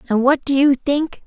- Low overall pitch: No, very high, 275 Hz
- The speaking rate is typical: No, fast, 235 wpm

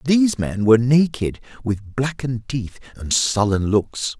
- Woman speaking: No, male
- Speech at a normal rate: Yes, average, 145 wpm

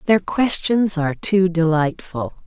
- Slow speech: Yes, slow, 120 wpm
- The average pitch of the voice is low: No, medium, 175 Hz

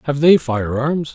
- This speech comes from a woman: No, male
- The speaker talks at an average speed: No, fast, 210 wpm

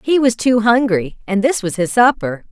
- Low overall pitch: No, high, 225 Hz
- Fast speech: Yes, fast, 215 wpm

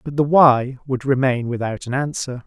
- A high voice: No, low, 130 Hz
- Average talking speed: Yes, average, 195 wpm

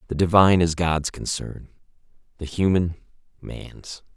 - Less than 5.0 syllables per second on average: Yes, 4.4 syllables/s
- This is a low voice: Yes, very low, 85 Hz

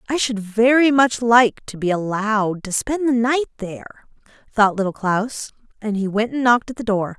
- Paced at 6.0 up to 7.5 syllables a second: No, 5.0 syllables/s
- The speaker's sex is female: Yes, female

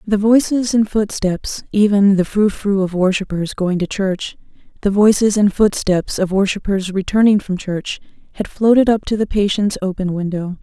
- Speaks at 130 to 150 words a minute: No, average, 170 wpm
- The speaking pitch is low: No, high, 200 Hz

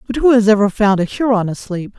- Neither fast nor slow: No, fast, 240 wpm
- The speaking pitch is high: Yes, high, 215 Hz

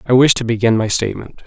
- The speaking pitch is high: No, low, 120 Hz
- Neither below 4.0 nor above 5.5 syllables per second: No, 6.7 syllables/s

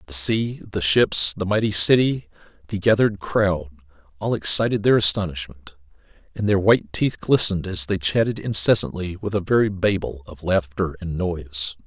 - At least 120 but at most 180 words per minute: Yes, average, 155 wpm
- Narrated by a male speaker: Yes, male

